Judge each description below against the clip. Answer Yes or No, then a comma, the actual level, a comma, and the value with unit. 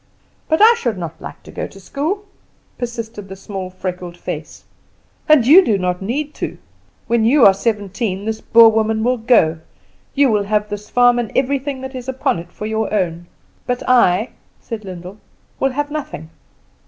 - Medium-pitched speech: No, high, 220 Hz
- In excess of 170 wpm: Yes, average, 180 wpm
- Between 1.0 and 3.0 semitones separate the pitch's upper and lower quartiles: No, average, 4.9 semitones